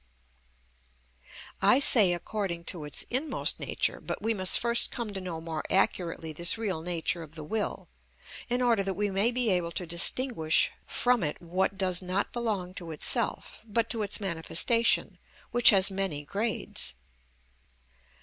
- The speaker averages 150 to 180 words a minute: Yes, average, 155 wpm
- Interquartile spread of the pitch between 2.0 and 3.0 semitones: No, average, 4.9 semitones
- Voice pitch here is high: Yes, high, 195 Hz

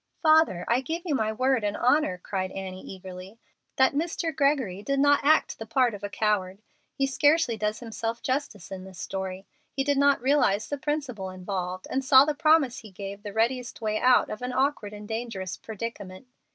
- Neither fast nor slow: Yes, average, 195 wpm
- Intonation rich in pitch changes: Yes, wide, 5.9 semitones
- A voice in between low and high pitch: No, high, 230 Hz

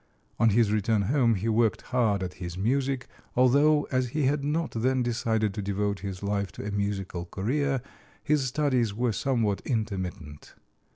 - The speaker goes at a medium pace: Yes, average, 165 wpm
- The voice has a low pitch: Yes, low, 115 Hz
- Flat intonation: No, average, 4.5 semitones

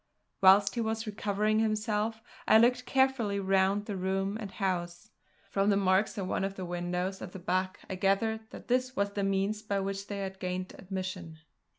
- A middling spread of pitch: No, narrow, 2.2 semitones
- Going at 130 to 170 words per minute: No, average, 190 wpm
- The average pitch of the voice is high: Yes, high, 195 Hz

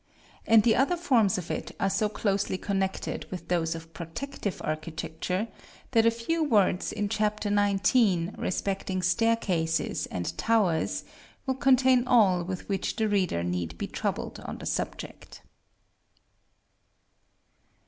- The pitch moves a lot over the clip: No, average, 4.4 semitones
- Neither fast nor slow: No, slow, 130 wpm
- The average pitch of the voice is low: No, high, 200 Hz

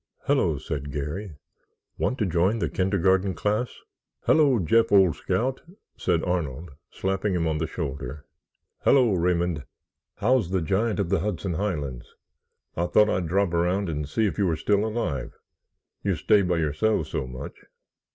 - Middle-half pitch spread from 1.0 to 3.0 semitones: No, average, 4.6 semitones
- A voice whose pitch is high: No, very low, 90 Hz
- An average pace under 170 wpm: Yes, average, 150 wpm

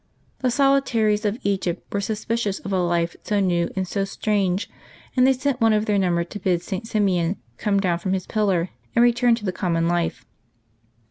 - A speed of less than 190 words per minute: No, average, 200 wpm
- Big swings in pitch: No, average, 3.6 semitones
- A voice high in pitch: Yes, high, 200 Hz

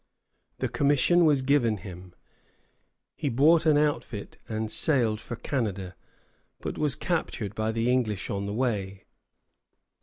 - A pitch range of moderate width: No, wide, 5.9 semitones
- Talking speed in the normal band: No, slow, 130 wpm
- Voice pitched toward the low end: Yes, low, 115 Hz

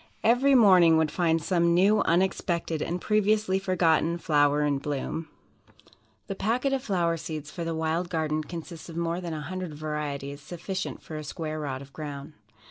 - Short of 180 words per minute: Yes, average, 170 wpm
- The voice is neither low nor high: Yes, medium, 165 Hz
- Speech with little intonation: No, average, 3.3 semitones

